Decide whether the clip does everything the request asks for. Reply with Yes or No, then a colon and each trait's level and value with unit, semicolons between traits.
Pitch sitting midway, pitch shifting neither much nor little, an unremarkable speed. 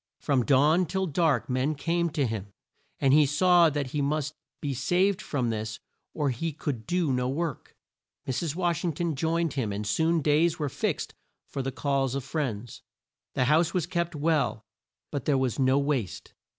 Yes: medium, 145 Hz; average, 4.1 semitones; average, 180 wpm